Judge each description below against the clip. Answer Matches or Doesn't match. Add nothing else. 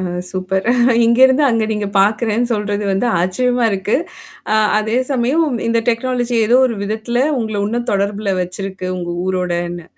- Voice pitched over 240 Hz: Doesn't match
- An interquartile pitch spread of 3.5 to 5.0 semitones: Matches